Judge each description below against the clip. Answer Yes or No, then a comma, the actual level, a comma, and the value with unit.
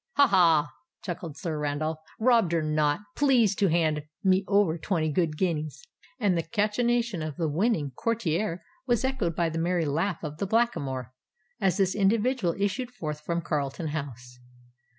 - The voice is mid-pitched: Yes, medium, 170 Hz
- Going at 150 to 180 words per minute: Yes, average, 155 wpm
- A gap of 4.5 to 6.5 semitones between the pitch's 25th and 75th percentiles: Yes, average, 5.2 semitones